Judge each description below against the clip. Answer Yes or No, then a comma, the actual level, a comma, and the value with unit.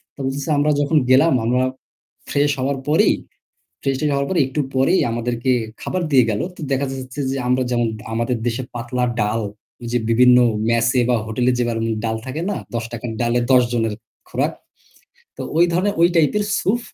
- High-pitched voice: No, low, 130 Hz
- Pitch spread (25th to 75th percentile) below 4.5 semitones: Yes, average, 3.3 semitones